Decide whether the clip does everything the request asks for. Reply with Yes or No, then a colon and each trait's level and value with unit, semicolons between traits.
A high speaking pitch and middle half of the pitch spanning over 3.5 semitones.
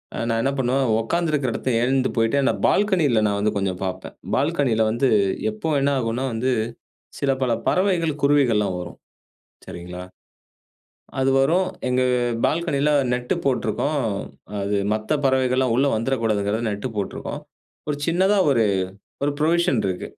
No: low, 130 Hz; average, 4.7 semitones